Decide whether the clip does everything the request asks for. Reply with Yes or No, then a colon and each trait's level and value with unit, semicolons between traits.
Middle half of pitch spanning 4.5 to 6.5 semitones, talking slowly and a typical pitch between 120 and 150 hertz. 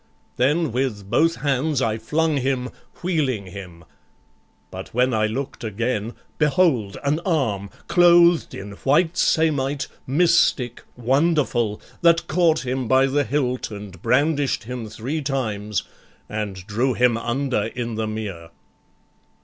Yes: wide, 5.4 semitones; slow, 125 wpm; low, 130 Hz